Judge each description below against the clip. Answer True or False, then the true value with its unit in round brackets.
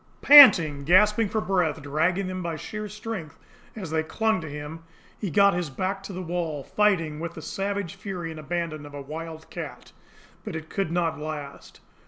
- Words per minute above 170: True (185 wpm)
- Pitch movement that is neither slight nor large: True (3.9 semitones)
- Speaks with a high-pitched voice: False (170 Hz)